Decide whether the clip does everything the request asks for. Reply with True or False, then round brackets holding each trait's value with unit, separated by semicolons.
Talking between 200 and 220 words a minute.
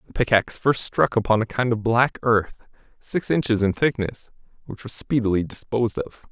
False (180 wpm)